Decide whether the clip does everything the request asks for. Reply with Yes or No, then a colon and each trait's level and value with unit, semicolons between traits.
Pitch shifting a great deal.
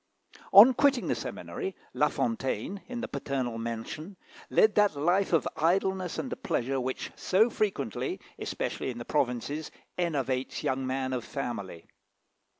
Yes: wide, 7.8 semitones